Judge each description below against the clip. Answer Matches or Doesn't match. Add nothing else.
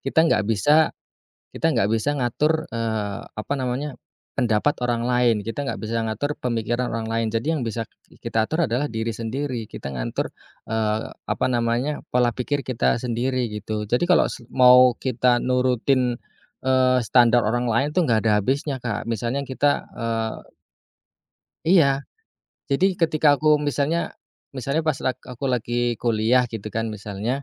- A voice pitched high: Doesn't match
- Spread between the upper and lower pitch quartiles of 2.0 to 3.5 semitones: Matches